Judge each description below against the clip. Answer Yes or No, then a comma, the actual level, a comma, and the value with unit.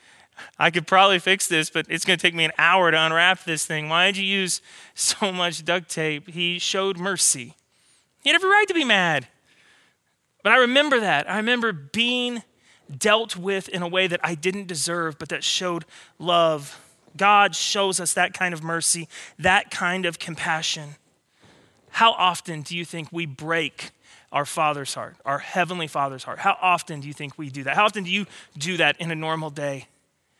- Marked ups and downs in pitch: No, average, 3.3 semitones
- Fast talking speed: No, average, 190 wpm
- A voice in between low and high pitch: Yes, medium, 175 Hz